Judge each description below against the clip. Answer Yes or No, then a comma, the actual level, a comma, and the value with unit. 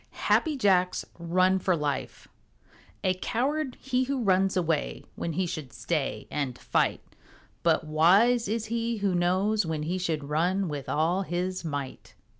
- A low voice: No, medium, 185 Hz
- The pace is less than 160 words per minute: Yes, average, 150 wpm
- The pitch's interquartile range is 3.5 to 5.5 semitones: Yes, average, 4.6 semitones